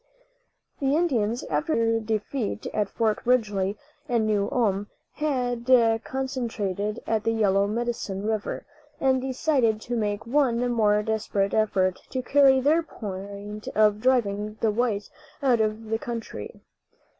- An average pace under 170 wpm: Yes, slow, 135 wpm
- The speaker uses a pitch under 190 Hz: No, high, 225 Hz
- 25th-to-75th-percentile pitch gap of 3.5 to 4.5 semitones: No, average, 3.1 semitones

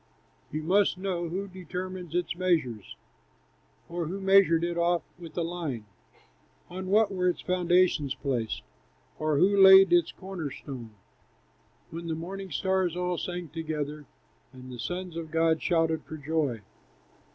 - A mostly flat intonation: No, average, 3.1 semitones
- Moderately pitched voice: Yes, medium, 170 Hz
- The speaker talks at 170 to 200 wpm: No, average, 145 wpm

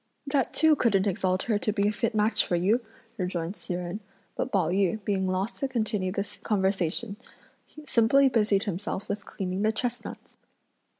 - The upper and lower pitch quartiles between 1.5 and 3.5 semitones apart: Yes, average, 3.1 semitones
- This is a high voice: Yes, high, 205 Hz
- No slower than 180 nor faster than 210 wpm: No, average, 170 wpm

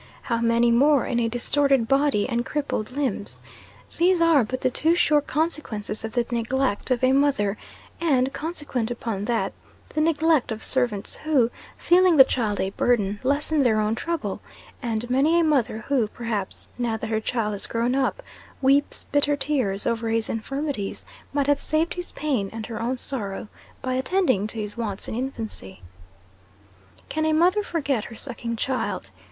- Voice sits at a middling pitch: No, very high, 255 Hz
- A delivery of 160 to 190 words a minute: Yes, average, 170 wpm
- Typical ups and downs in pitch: Yes, average, 4.5 semitones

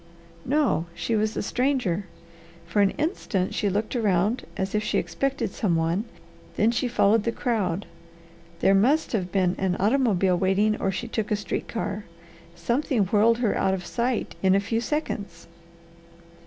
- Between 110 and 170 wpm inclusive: Yes, average, 165 wpm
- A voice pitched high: Yes, high, 210 Hz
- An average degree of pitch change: Yes, average, 3.7 semitones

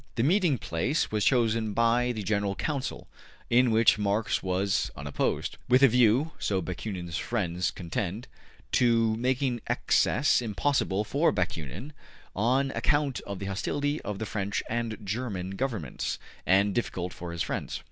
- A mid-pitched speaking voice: No, low, 110 Hz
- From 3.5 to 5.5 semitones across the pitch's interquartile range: Yes, average, 4.6 semitones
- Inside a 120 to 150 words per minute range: Yes, average, 145 wpm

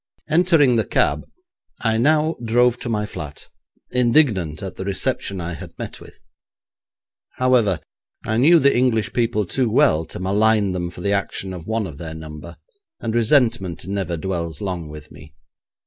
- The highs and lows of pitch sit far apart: Yes, wide, 6.0 semitones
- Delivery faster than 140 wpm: Yes, average, 165 wpm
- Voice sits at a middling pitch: No, low, 100 Hz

